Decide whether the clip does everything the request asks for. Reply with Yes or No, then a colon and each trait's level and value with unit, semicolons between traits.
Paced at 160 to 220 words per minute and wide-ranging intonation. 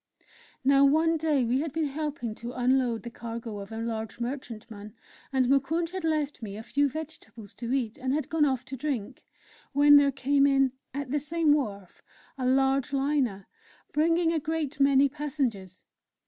No: average, 175 wpm; average, 3.9 semitones